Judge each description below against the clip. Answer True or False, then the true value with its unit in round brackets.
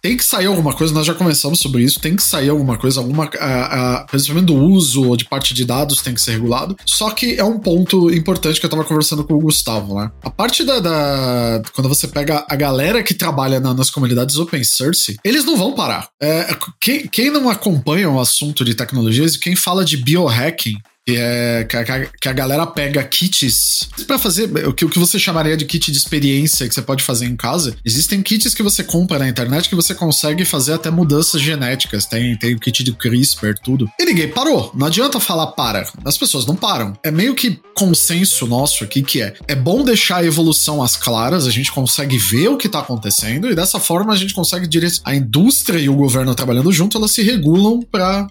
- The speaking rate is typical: False (215 wpm)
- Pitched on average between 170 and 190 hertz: False (150 Hz)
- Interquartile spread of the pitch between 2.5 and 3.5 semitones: False (5.6 semitones)